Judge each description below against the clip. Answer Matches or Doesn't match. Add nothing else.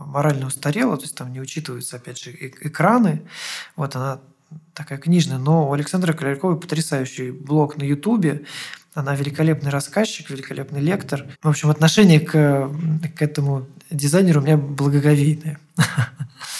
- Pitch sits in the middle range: Matches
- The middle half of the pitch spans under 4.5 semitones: Matches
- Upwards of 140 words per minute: Doesn't match